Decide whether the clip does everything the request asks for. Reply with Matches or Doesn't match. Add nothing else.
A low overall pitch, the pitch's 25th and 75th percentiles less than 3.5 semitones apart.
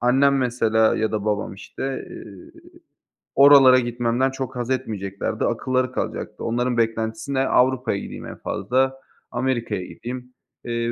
Matches